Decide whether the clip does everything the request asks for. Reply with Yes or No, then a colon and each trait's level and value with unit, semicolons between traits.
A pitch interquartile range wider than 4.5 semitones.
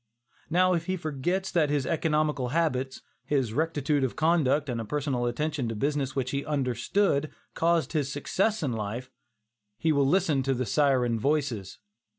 No: average, 3.6 semitones